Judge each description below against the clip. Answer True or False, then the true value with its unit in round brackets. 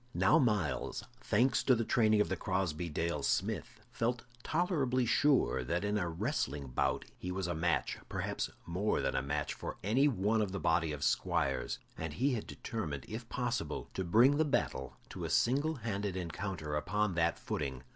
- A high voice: False (100 Hz)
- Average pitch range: False (6.6 semitones)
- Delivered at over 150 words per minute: True (180 wpm)